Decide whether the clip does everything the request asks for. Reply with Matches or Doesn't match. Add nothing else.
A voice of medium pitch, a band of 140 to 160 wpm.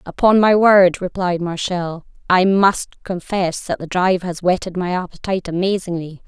Matches